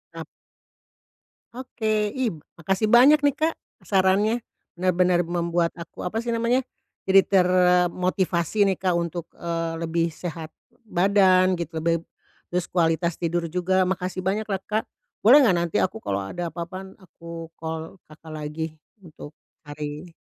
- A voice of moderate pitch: Yes, medium, 180 Hz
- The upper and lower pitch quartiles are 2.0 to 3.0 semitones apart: Yes, average, 2.7 semitones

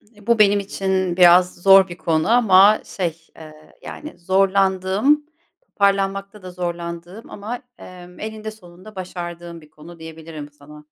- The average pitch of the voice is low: No, medium, 185 Hz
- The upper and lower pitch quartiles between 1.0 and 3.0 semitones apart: Yes, average, 2.7 semitones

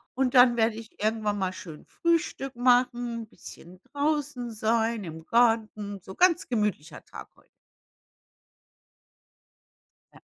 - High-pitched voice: Yes, high, 230 Hz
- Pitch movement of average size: Yes, average, 3.1 semitones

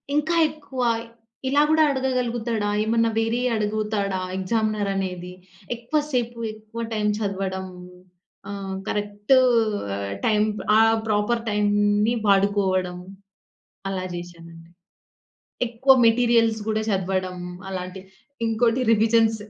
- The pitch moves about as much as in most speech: Yes, average, 3.1 semitones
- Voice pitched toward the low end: No, high, 215 Hz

